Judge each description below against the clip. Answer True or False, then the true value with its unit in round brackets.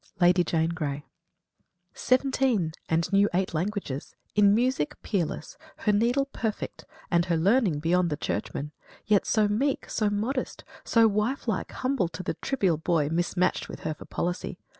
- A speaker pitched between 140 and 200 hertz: True (190 Hz)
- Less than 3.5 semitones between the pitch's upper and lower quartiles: False (5.0 semitones)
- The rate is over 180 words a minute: False (160 wpm)